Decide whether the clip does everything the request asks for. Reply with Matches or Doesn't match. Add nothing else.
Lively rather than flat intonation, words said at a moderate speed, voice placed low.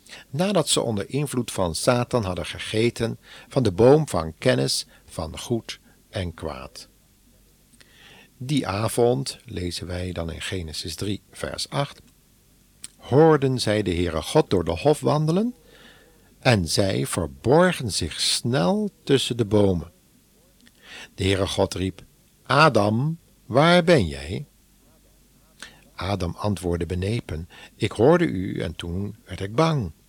Doesn't match